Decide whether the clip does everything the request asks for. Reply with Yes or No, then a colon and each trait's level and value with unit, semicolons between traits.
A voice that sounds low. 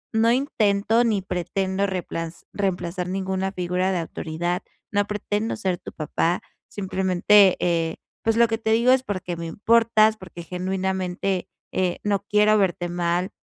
No: high, 190 Hz